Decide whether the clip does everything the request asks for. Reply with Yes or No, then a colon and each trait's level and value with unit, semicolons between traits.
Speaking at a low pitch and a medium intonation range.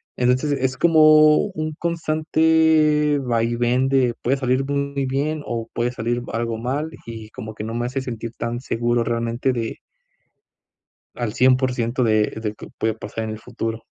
Yes: low, 125 Hz; average, 3.6 semitones